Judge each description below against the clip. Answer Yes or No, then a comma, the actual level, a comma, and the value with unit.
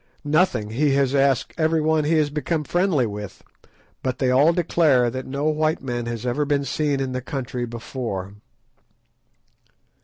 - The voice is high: No, low, 135 Hz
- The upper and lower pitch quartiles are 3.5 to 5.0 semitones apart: Yes, average, 3.8 semitones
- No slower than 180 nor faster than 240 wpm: No, average, 155 wpm